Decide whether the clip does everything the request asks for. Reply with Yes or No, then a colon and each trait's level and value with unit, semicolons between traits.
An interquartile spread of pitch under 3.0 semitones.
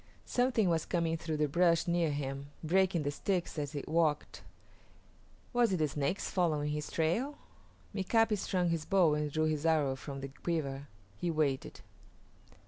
No: average, 3.3 semitones